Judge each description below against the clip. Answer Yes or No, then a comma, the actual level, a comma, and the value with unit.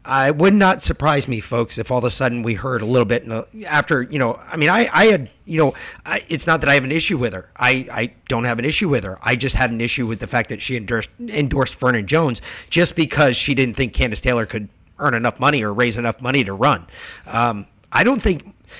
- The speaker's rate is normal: No, fast, 250 wpm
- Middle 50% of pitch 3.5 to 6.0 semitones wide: Yes, average, 4.1 semitones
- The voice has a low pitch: Yes, low, 125 Hz